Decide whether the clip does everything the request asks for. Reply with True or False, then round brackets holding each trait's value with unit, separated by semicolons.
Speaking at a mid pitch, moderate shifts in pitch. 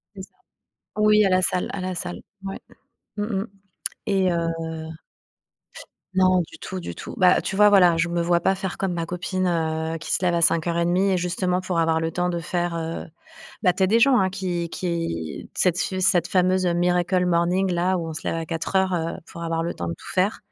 False (180 Hz; 1.9 semitones)